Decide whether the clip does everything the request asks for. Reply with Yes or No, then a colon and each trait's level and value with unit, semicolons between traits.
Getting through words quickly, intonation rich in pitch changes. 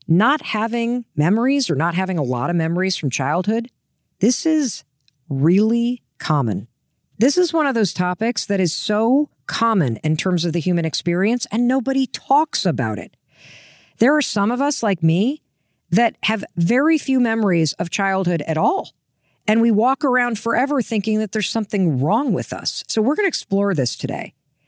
No: average, 175 wpm; wide, 6.2 semitones